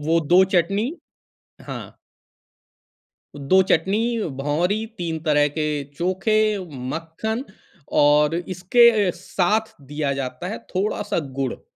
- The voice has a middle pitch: Yes, medium, 175 Hz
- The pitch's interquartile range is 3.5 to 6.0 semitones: Yes, average, 5.2 semitones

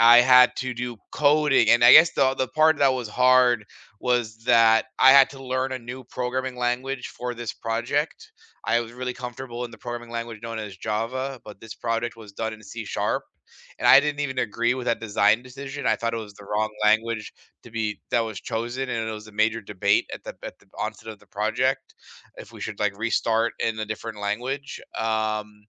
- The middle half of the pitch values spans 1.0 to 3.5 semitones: Yes, average, 2.8 semitones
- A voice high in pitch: No, low, 120 Hz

